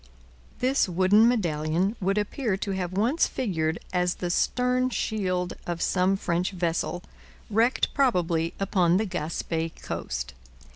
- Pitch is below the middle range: No, medium, 185 Hz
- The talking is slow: Yes, slow, 130 wpm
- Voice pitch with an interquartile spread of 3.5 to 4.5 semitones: Yes, average, 4.0 semitones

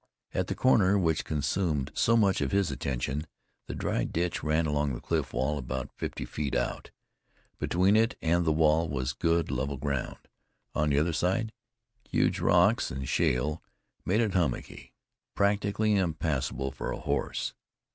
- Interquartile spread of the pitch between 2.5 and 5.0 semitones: No, wide, 5.4 semitones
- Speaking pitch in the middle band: No, very low, 80 Hz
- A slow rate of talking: No, average, 155 wpm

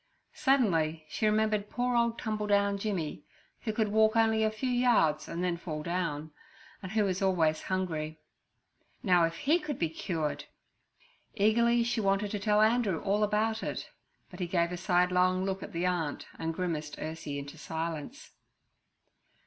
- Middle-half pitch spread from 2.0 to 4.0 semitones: No, average, 4.7 semitones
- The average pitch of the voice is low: No, high, 190 Hz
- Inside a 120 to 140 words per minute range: No, average, 160 wpm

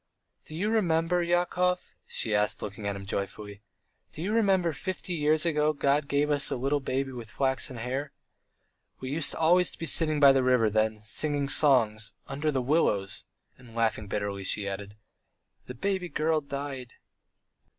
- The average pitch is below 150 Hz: Yes, medium, 140 Hz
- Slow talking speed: No, average, 165 wpm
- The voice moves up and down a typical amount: No, wide, 6.3 semitones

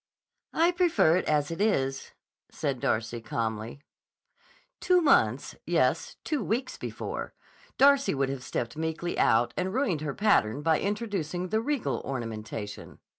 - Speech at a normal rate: No, slow, 125 wpm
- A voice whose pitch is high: No, medium, 160 Hz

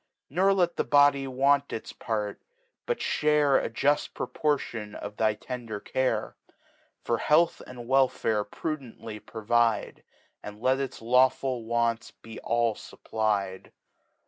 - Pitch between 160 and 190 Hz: No, low, 120 Hz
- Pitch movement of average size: Yes, average, 4.0 semitones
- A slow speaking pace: Yes, slow, 125 wpm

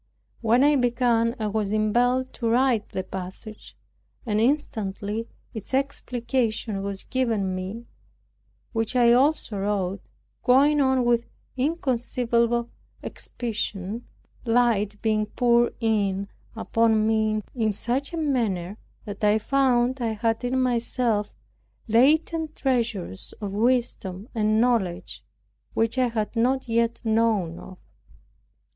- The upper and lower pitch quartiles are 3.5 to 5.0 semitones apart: No, average, 2.8 semitones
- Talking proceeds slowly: Yes, slow, 115 wpm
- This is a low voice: No, high, 230 Hz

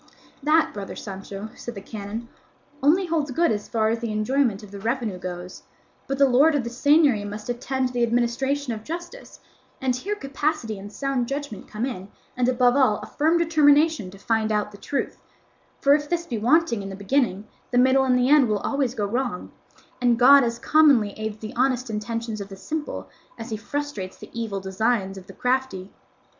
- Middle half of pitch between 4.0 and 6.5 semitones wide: Yes, average, 4.8 semitones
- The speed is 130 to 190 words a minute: No, average, 200 wpm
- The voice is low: No, high, 245 Hz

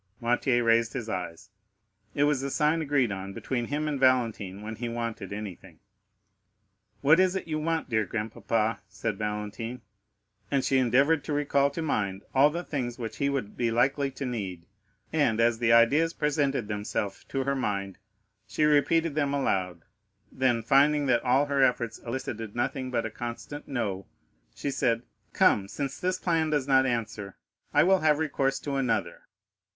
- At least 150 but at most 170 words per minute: Yes, average, 165 wpm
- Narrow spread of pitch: No, average, 4.5 semitones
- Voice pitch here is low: Yes, low, 125 Hz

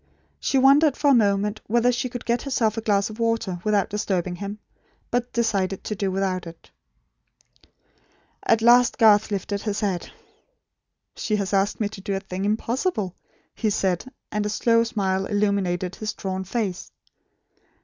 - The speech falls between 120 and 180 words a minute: Yes, average, 160 wpm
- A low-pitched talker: No, high, 210 Hz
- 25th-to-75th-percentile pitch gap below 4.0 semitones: Yes, average, 3.0 semitones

